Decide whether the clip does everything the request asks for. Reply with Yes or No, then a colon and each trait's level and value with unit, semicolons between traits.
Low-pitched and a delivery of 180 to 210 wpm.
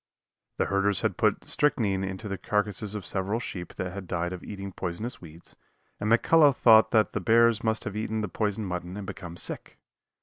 Yes: low, 100 Hz; average, 190 wpm